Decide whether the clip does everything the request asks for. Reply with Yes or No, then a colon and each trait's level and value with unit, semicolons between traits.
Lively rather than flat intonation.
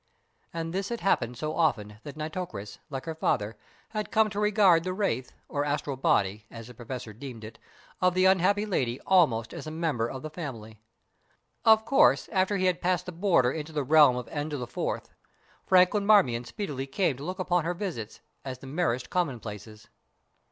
Yes: wide, 6.9 semitones